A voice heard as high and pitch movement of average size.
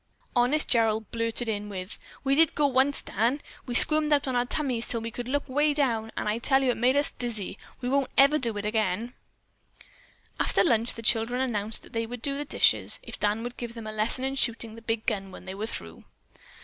Yes: high, 235 Hz; average, 3.5 semitones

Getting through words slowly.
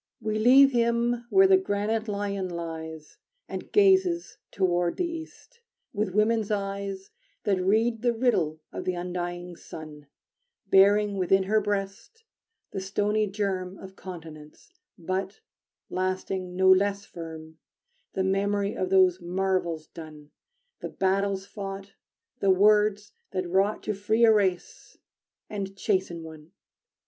Yes: slow, 130 wpm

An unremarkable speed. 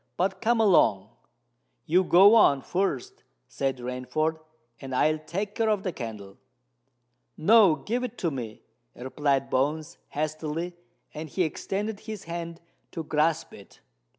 No: slow, 130 wpm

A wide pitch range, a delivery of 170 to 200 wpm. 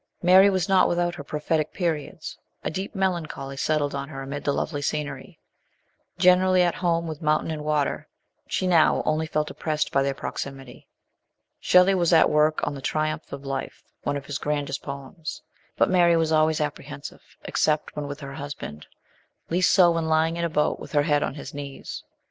No: average, 3.1 semitones; average, 190 wpm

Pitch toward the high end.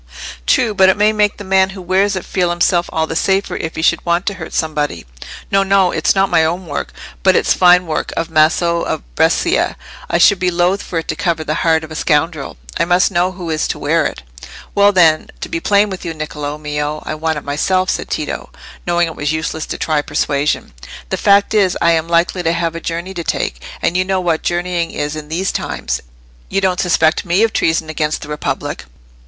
No: medium, 170 Hz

